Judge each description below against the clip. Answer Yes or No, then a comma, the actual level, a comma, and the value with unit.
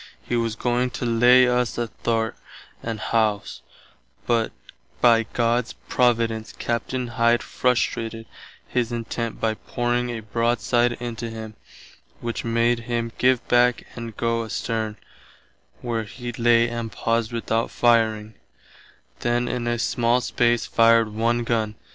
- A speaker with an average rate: No, slow, 130 wpm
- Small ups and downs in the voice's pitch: Yes, narrow, 1.1 semitones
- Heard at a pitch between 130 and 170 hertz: No, low, 115 Hz